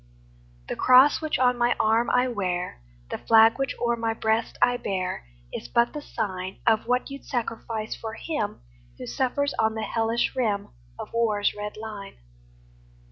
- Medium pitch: No, high, 225 Hz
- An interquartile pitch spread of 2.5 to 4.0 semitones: Yes, average, 2.8 semitones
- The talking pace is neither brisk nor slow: Yes, average, 170 wpm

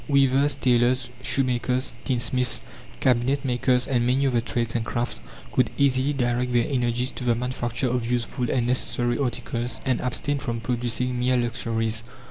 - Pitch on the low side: Yes, low, 125 Hz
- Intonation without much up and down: Yes, narrow, 1.4 semitones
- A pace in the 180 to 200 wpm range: No, average, 150 wpm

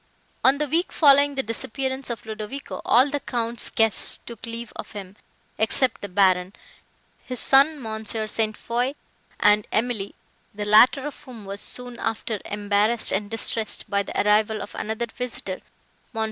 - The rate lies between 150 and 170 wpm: Yes, average, 160 wpm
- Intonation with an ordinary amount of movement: Yes, average, 3.5 semitones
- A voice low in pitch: No, high, 225 Hz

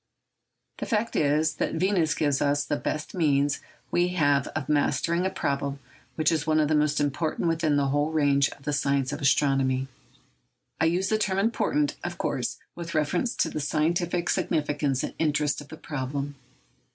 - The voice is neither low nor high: Yes, medium, 150 Hz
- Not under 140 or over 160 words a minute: No, average, 175 wpm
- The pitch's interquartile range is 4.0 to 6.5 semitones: No, average, 2.8 semitones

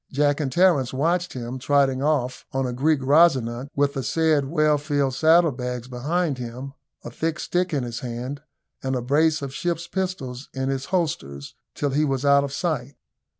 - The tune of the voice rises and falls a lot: No, average, 3.3 semitones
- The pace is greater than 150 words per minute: Yes, average, 185 wpm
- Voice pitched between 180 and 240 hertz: No, medium, 140 Hz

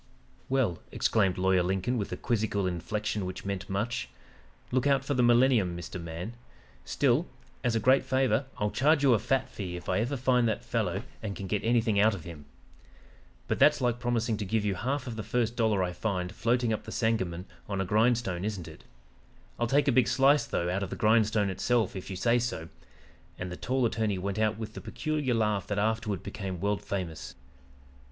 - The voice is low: Yes, low, 110 Hz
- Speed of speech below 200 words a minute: No, fast, 205 wpm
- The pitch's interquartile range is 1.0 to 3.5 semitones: No, average, 4.2 semitones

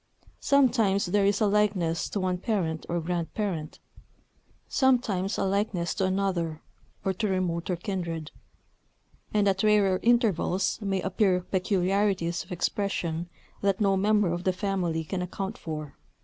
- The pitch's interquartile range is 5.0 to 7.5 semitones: No, average, 2.7 semitones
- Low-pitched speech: No, high, 190 Hz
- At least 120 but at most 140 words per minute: Yes, slow, 135 wpm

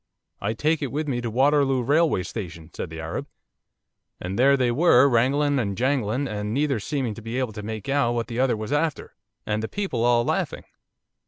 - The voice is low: Yes, low, 120 Hz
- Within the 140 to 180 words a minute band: No, average, 200 wpm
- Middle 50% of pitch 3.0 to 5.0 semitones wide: Yes, average, 4.5 semitones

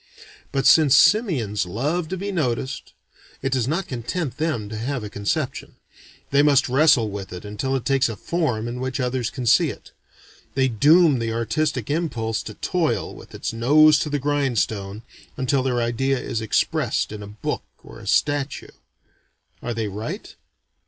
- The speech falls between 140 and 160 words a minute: No, average, 170 wpm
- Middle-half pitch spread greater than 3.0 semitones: Yes, average, 4.6 semitones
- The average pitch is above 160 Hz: No, low, 130 Hz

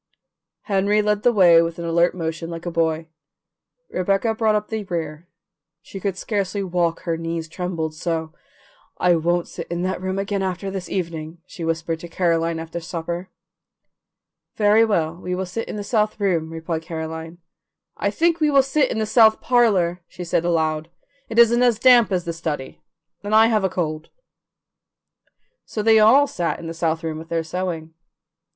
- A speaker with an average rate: Yes, average, 180 wpm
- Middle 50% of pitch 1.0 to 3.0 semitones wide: No, average, 4.0 semitones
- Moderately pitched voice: Yes, medium, 175 Hz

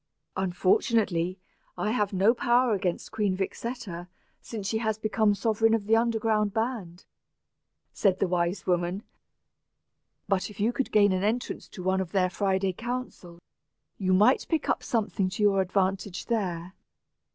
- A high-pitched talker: Yes, high, 200 Hz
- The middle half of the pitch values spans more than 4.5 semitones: No, average, 3.2 semitones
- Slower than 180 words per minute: Yes, average, 150 wpm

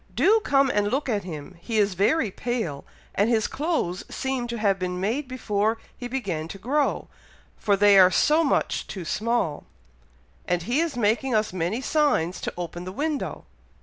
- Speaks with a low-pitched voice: No, high, 215 Hz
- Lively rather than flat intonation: Yes, wide, 6.2 semitones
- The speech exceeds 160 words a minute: Yes, average, 180 wpm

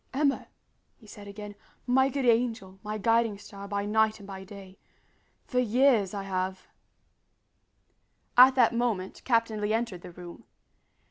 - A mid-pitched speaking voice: No, high, 215 Hz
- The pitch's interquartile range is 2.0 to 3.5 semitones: Yes, average, 3.2 semitones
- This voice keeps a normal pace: Yes, average, 150 wpm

